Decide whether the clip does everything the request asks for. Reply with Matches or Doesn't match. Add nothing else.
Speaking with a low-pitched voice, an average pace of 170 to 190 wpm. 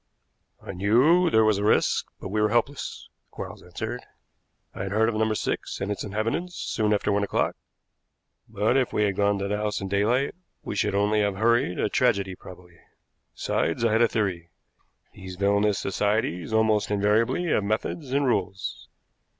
Matches